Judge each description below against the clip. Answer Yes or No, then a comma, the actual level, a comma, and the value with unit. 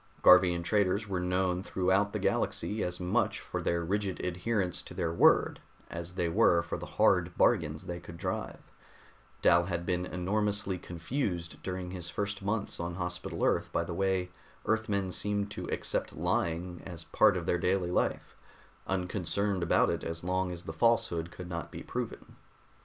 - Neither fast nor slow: Yes, average, 170 wpm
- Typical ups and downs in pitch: No, narrow, 2.2 semitones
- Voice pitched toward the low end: Yes, very low, 90 Hz